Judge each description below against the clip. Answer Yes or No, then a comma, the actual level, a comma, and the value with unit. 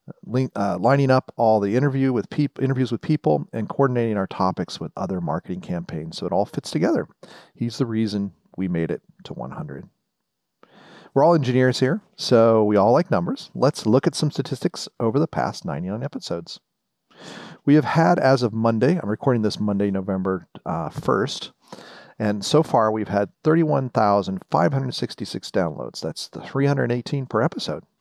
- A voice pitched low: Yes, low, 120 Hz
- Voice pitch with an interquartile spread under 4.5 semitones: No, average, 4.9 semitones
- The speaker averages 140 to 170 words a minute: Yes, average, 165 wpm